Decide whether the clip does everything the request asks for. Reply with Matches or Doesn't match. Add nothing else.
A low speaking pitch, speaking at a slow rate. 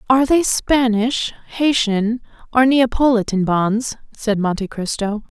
Doesn't match